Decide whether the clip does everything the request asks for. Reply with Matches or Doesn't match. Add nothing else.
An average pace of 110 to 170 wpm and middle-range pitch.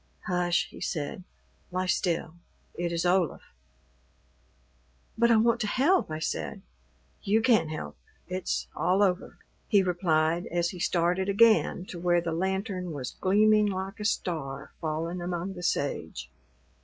Matches